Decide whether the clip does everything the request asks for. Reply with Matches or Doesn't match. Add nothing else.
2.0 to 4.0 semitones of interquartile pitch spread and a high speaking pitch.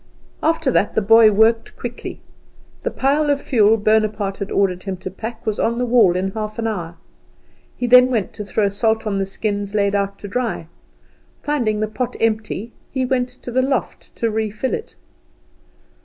Matches